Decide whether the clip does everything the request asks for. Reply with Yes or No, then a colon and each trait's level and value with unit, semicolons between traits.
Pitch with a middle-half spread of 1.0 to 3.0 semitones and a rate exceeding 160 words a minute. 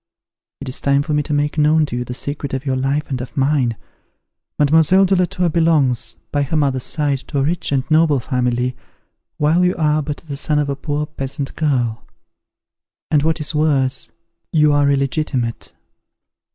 Yes: narrow, 2.5 semitones; average, 185 wpm